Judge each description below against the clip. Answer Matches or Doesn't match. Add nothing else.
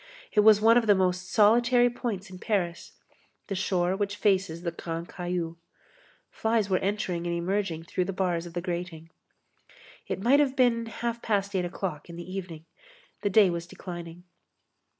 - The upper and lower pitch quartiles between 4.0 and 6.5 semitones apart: Doesn't match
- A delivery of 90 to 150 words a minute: Doesn't match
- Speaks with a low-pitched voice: Doesn't match